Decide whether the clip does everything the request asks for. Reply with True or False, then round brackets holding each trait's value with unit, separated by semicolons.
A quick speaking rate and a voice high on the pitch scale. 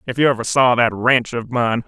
False (255 wpm; 120 Hz)